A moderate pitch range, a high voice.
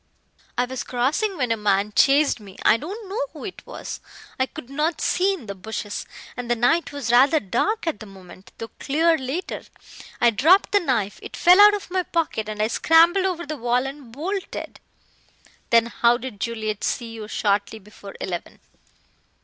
No: wide, 7.3 semitones; very high, 255 Hz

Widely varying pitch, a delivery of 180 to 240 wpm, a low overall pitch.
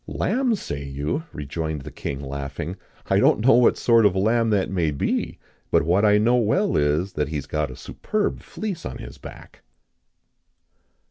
Yes: wide, 8.0 semitones; average, 185 wpm; very low, 90 Hz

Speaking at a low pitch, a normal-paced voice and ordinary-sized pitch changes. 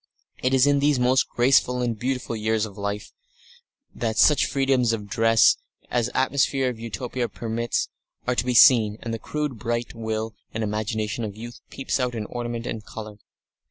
No: low, 120 Hz; average, 180 wpm; narrow, 2.3 semitones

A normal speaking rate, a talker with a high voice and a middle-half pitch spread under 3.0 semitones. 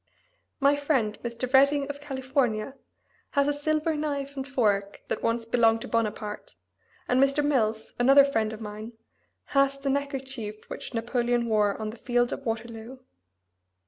No: average, 150 wpm; very high, 250 Hz; average, 3.8 semitones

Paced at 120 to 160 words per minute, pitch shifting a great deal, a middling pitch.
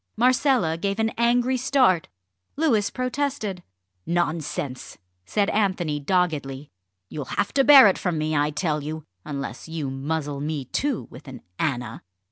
Yes: average, 140 wpm; wide, 8.1 semitones; medium, 175 Hz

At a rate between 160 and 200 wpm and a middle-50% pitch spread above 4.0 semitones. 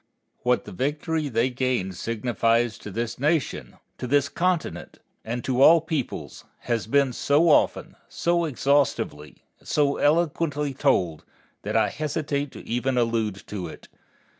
No: average, 140 wpm; average, 4.4 semitones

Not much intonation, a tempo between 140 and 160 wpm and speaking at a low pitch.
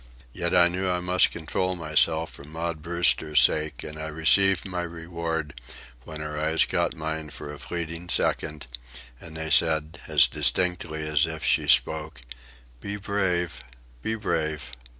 Yes: narrow, 2.2 semitones; average, 150 wpm; very low, 80 Hz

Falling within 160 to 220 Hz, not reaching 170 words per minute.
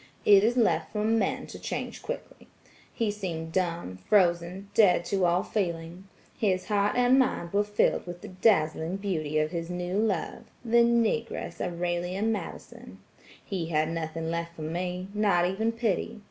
Yes: medium, 185 Hz; average, 150 wpm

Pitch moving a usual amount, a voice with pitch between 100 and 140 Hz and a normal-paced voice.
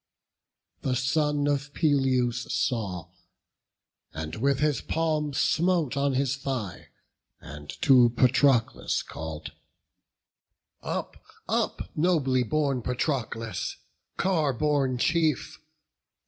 No: average, 3.4 semitones; low, 135 Hz; slow, 90 wpm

